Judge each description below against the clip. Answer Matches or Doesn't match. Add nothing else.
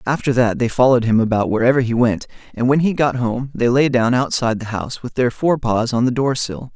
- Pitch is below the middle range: Matches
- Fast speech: Matches